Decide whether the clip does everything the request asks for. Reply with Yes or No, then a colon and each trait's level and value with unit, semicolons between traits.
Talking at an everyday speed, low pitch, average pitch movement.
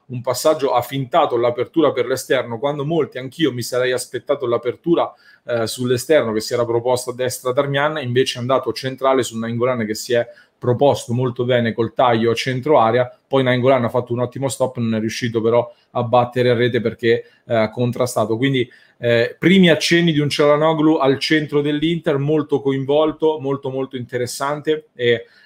No: fast, 175 wpm; low, 125 Hz; average, 3.0 semitones